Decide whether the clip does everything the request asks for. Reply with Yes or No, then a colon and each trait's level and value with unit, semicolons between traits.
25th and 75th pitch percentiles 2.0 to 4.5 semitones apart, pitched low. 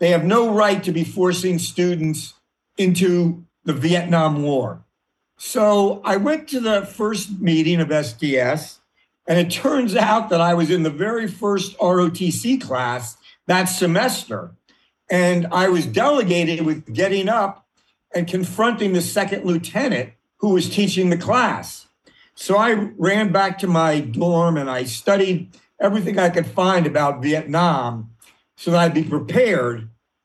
No: average, 3.7 semitones; medium, 180 Hz